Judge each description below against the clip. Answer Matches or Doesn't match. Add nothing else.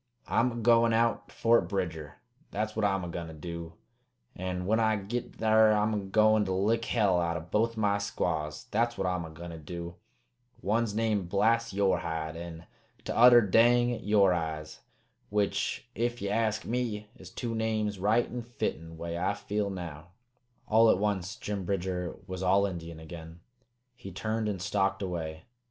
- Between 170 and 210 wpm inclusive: Matches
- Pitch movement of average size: Matches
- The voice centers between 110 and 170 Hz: Doesn't match